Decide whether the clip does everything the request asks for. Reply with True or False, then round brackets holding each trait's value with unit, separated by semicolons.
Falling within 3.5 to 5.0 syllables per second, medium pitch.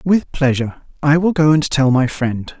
True (4.8 syllables/s; 145 Hz)